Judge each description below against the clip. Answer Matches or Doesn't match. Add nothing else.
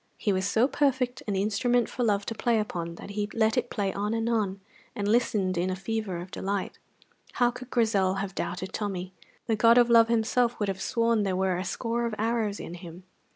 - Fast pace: Matches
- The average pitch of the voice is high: Matches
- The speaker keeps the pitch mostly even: Doesn't match